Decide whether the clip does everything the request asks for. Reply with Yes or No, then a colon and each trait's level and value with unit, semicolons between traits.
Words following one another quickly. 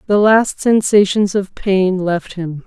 No: average, 155 wpm